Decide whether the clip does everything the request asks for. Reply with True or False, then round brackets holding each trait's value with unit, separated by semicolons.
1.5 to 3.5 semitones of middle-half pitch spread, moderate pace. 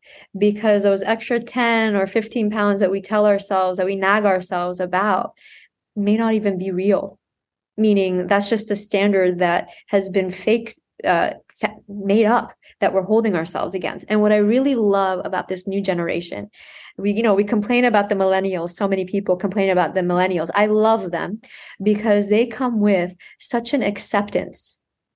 True (2.4 semitones; 170 wpm)